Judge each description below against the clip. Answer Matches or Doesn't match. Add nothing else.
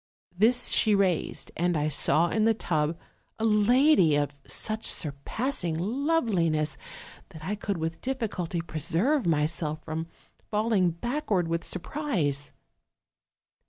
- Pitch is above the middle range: Doesn't match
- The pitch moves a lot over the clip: Matches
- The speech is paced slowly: Matches